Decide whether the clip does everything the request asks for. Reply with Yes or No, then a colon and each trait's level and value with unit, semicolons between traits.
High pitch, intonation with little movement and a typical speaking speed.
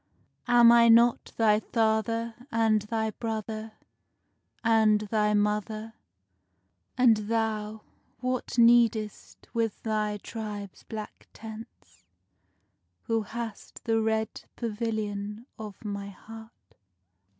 No: high, 220 Hz; narrow, 1.3 semitones; slow, 95 wpm